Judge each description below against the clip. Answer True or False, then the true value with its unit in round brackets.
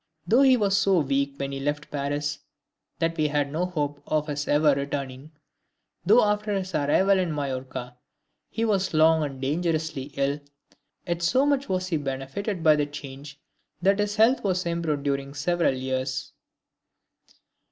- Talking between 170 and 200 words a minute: False (160 wpm)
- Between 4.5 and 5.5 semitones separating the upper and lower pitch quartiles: True (4.8 semitones)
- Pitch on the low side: False (150 Hz)